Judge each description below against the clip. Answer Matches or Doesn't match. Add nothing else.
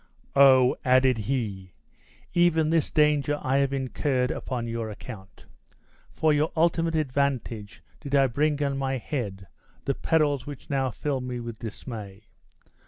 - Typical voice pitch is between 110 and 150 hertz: Matches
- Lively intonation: Doesn't match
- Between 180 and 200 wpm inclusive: Doesn't match